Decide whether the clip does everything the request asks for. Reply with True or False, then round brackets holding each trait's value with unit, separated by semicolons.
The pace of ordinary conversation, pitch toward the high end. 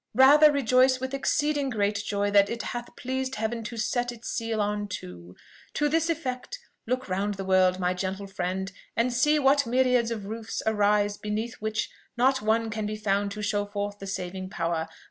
True (185 wpm; 215 Hz)